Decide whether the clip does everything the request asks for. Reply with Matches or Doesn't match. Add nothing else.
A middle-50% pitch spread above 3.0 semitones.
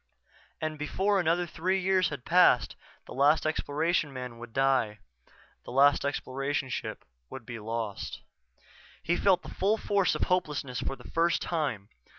Matches